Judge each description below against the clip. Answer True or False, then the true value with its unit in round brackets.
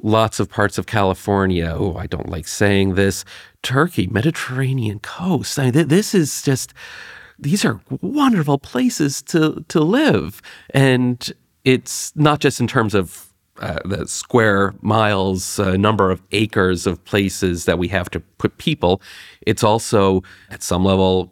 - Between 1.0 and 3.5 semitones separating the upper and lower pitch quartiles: False (5.6 semitones)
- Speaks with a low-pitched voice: True (105 Hz)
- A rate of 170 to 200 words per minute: False (155 wpm)